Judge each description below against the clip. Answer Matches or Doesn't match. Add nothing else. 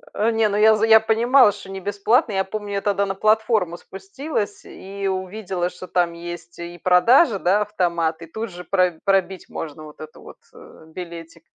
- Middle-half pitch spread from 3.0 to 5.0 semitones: Matches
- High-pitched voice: Matches